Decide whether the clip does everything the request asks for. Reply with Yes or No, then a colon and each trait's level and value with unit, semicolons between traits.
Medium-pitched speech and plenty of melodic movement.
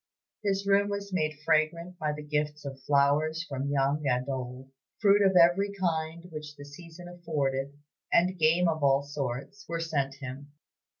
No: medium, 155 Hz; average, 3.7 semitones